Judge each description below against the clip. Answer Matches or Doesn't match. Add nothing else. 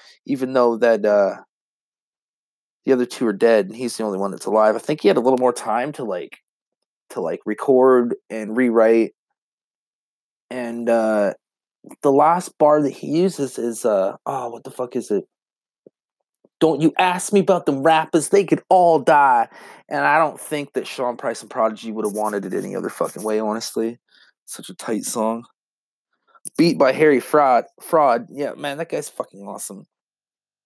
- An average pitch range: Doesn't match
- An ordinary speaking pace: Matches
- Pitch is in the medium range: Doesn't match